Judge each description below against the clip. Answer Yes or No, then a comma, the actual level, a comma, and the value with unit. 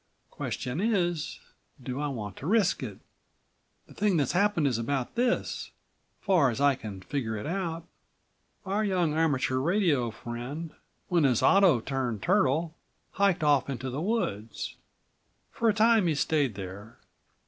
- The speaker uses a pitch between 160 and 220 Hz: No, medium, 150 Hz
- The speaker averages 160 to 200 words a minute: No, average, 150 wpm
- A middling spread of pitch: No, wide, 6.9 semitones